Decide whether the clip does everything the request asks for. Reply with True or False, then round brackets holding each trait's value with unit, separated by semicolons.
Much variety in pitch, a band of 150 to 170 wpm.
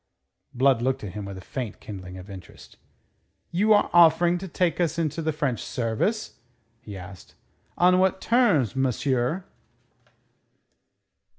False (7.9 semitones; 135 wpm)